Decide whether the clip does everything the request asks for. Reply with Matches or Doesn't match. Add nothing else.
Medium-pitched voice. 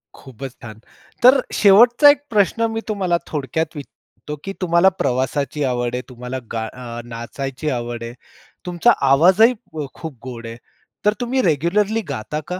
Matches